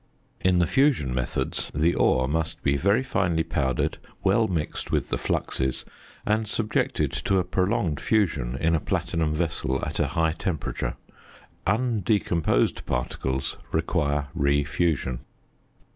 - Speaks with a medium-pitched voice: No, very low, 80 Hz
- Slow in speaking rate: Yes, slow, 130 wpm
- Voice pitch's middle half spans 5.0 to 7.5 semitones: Yes, average, 5.3 semitones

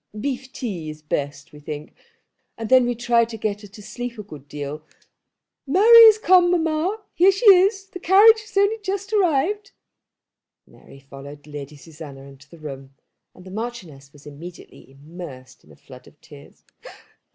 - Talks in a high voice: Yes, high, 210 Hz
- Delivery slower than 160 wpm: No, average, 170 wpm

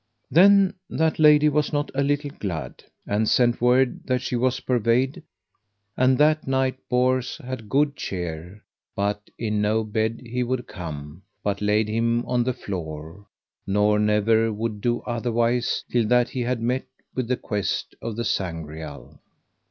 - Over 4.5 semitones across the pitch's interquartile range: No, average, 3.8 semitones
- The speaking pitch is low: Yes, low, 120 Hz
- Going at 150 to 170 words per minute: Yes, average, 155 wpm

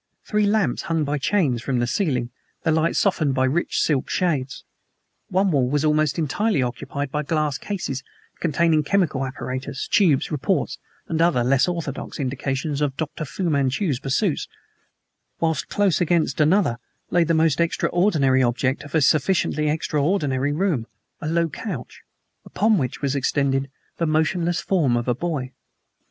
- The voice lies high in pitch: No, medium, 150 Hz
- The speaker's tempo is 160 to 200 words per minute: No, average, 150 wpm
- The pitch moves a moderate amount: Yes, average, 4.1 semitones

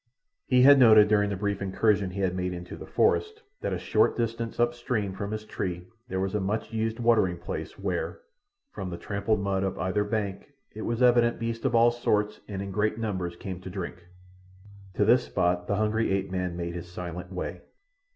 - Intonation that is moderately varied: Yes, average, 3.6 semitones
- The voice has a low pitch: Yes, low, 100 Hz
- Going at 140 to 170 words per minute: No, fast, 205 wpm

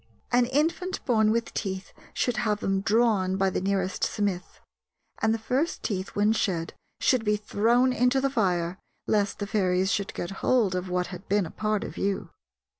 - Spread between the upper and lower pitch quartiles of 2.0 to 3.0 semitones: No, average, 3.6 semitones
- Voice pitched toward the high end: Yes, high, 210 Hz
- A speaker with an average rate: Yes, average, 180 wpm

